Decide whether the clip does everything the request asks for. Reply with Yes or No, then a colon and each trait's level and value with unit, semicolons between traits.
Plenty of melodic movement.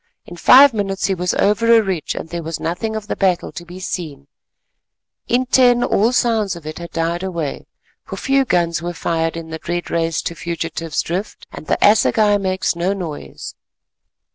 No: average, 4.0 semitones